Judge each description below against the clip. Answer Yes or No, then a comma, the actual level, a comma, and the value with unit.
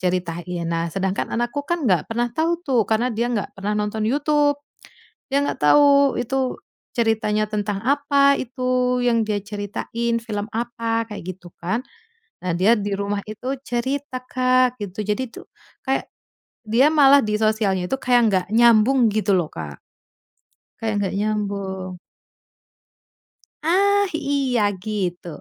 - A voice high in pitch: Yes, high, 225 Hz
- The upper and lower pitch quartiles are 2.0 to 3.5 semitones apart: No, average, 4.1 semitones